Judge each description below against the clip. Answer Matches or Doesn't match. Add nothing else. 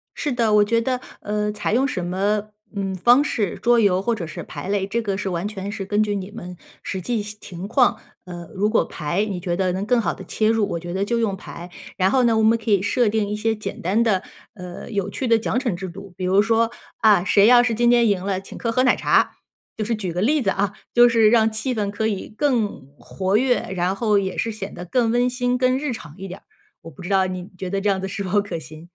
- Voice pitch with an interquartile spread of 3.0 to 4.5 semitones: Matches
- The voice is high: Matches